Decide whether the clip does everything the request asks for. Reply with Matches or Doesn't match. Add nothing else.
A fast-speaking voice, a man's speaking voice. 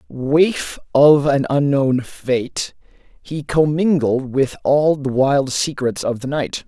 Doesn't match